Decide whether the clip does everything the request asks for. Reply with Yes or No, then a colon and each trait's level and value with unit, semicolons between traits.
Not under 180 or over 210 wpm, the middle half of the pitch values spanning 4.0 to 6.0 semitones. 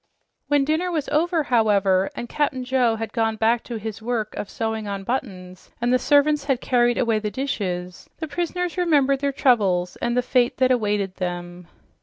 Yes: average, 185 wpm; average, 5.0 semitones